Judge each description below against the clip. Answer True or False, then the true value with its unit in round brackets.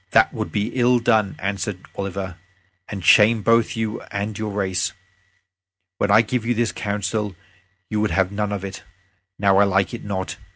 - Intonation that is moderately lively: False (2.1 semitones)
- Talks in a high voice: False (105 Hz)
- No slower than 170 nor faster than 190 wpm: True (175 wpm)